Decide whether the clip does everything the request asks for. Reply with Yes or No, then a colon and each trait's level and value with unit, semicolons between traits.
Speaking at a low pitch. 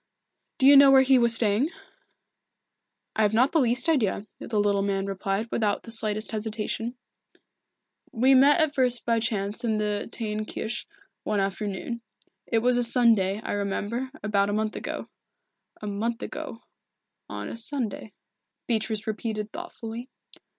No: high, 225 Hz